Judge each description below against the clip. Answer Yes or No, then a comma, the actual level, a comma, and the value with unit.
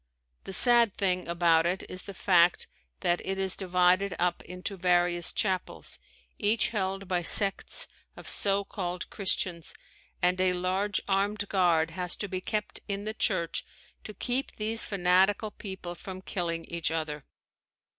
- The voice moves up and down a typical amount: No, narrow, 2.2 semitones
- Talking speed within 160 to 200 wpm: No, average, 150 wpm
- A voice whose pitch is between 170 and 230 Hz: Yes, medium, 185 Hz